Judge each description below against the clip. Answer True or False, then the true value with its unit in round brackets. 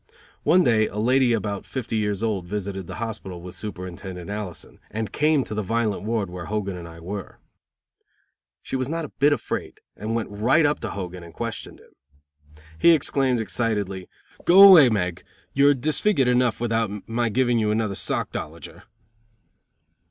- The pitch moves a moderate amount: True (4.4 semitones)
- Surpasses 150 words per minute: True (165 wpm)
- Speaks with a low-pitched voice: True (110 Hz)